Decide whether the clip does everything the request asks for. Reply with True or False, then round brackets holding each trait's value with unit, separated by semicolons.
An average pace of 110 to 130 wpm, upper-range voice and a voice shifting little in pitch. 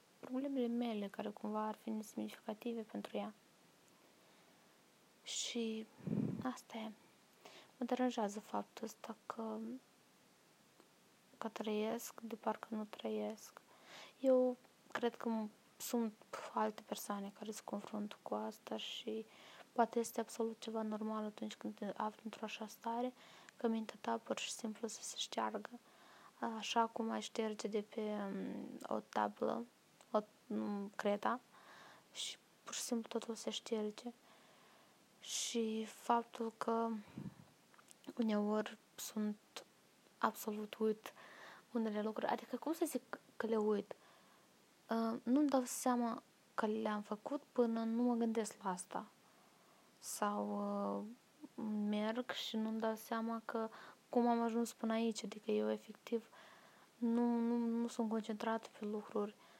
True (125 wpm; 225 Hz; 1.7 semitones)